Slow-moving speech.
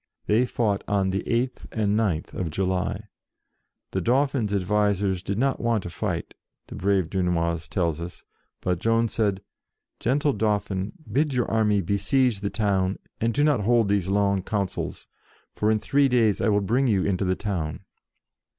No: average, 180 wpm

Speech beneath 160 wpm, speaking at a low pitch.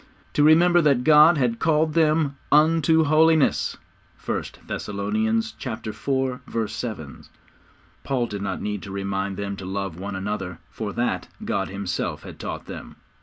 Yes: average, 140 wpm; low, 115 Hz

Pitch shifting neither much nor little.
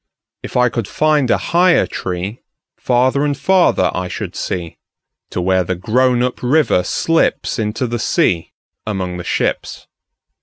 No: wide, 7.0 semitones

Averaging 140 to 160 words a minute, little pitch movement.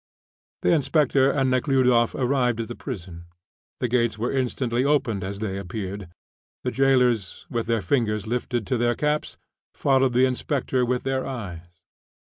No: average, 150 wpm; average, 3.3 semitones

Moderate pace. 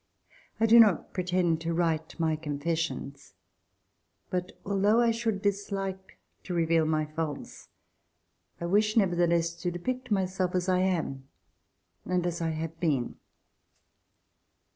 No: slow, 130 wpm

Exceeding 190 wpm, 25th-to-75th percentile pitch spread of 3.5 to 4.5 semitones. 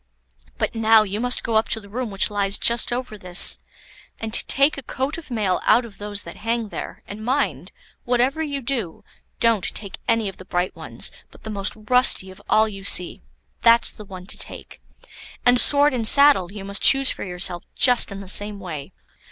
Yes: average, 200 wpm; average, 3.8 semitones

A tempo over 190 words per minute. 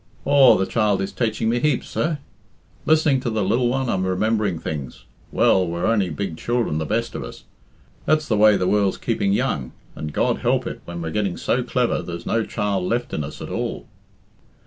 Yes: average, 200 wpm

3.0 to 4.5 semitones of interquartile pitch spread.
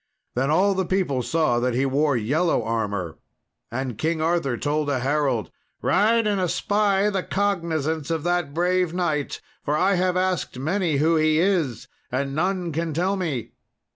No: average, 4.9 semitones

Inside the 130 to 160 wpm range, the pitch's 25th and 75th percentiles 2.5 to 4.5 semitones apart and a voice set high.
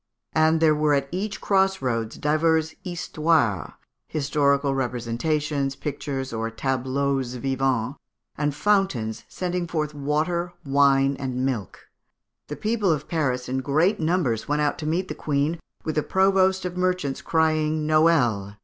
No: average, 140 wpm; average, 3.6 semitones; medium, 150 Hz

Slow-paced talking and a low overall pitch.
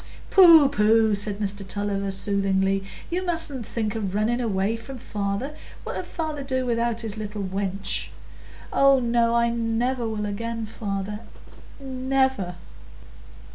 No: slow, 130 wpm; high, 225 Hz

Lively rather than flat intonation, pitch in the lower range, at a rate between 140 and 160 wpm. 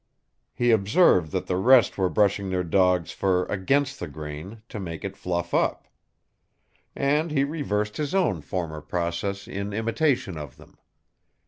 Yes: wide, 5.8 semitones; low, 100 Hz; average, 150 wpm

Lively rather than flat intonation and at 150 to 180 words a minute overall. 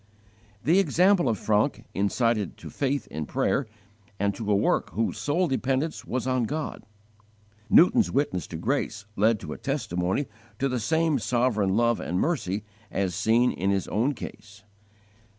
Yes: wide, 5.8 semitones; average, 155 wpm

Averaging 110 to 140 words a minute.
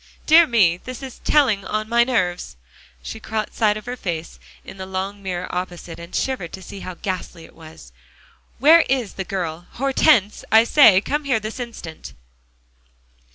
No: average, 170 wpm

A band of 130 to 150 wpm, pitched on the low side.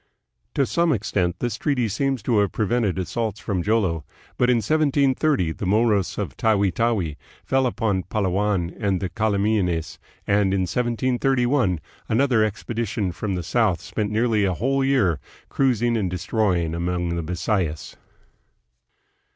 Yes: average, 140 wpm; low, 105 Hz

